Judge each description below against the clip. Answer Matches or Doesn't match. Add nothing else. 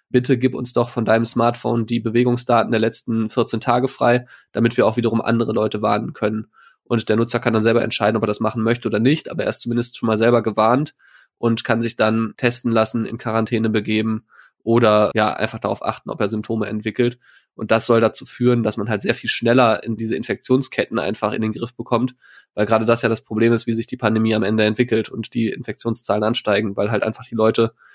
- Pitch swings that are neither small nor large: Doesn't match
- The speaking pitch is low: Matches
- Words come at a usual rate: Doesn't match